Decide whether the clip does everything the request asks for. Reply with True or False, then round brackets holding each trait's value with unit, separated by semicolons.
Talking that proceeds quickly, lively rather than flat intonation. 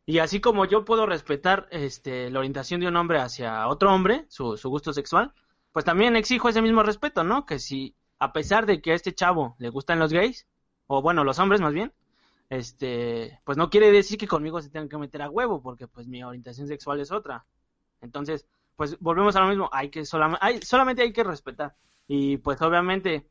True (210 wpm; 6.1 semitones)